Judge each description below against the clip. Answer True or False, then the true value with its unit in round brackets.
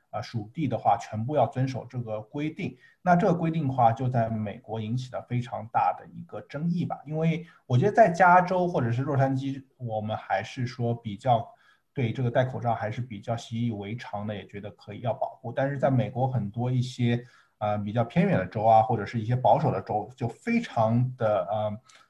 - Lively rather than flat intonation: False (3.6 semitones)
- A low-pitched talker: True (120 Hz)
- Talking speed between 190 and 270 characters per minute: False (310 characters per minute)